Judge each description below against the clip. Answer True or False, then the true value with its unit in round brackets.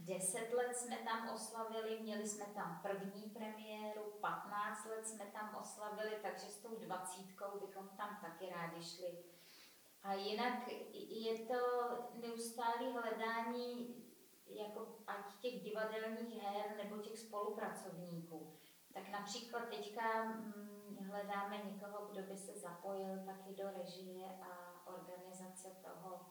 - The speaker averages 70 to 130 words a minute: True (120 wpm)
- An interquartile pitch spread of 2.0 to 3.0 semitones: True (2.7 semitones)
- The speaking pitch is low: False (205 Hz)